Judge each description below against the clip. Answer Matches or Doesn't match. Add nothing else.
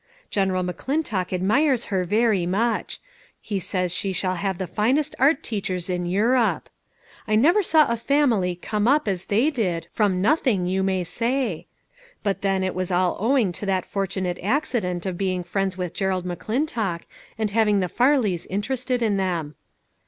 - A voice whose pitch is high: Matches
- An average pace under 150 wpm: Doesn't match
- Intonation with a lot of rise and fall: Doesn't match